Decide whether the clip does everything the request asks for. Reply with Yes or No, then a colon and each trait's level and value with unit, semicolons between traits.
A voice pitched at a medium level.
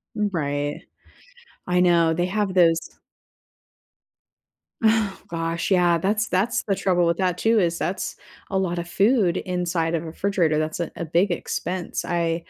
Yes: medium, 175 Hz